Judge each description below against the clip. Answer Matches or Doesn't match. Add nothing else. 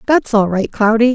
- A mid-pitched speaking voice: Doesn't match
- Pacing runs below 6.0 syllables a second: Matches